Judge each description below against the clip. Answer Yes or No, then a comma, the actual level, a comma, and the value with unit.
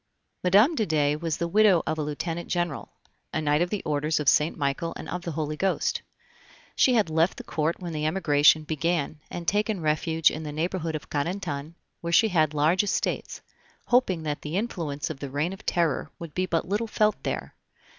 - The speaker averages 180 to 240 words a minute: Yes, average, 200 wpm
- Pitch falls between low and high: Yes, medium, 165 Hz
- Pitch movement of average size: Yes, average, 3.2 semitones